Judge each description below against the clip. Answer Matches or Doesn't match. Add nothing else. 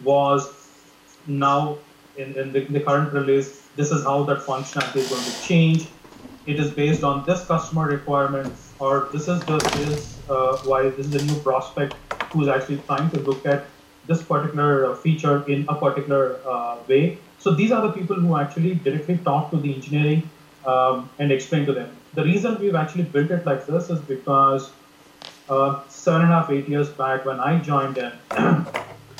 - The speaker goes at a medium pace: Matches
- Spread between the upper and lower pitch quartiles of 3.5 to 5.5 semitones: Doesn't match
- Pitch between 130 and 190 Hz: Matches